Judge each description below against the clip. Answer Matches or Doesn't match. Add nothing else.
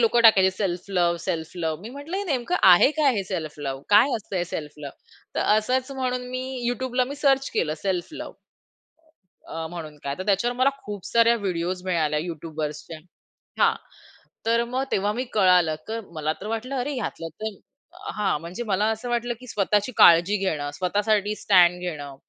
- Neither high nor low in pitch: Doesn't match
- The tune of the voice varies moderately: Doesn't match